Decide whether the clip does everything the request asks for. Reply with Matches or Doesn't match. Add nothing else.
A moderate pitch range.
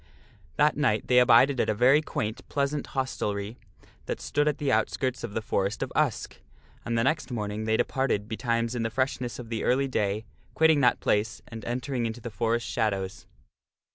Matches